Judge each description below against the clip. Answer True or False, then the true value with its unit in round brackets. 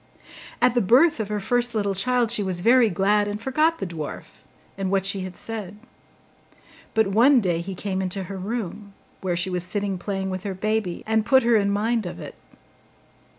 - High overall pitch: True (205 Hz)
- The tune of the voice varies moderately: True (3.3 semitones)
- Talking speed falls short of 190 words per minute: False (195 wpm)